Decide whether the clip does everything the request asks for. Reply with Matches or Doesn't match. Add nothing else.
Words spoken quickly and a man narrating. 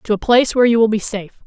Doesn't match